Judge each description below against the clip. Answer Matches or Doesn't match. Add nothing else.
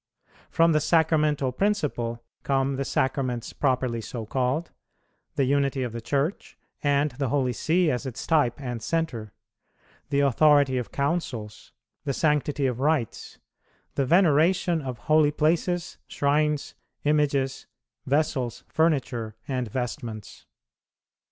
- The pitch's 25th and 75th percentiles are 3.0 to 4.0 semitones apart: Matches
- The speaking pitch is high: Doesn't match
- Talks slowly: Matches